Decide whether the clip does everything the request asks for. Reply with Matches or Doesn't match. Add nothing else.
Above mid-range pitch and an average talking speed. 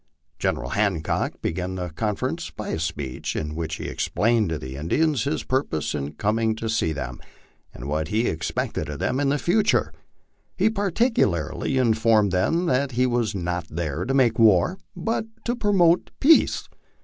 Doesn't match